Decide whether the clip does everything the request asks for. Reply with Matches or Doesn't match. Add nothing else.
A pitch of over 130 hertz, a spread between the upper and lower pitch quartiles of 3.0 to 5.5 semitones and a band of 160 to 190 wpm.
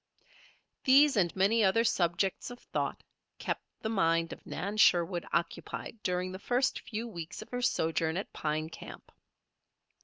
Doesn't match